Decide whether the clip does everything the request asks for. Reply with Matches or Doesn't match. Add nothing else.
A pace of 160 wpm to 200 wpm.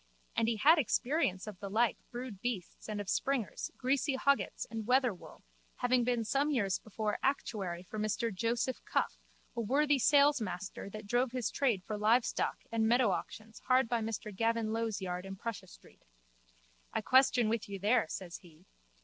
Matches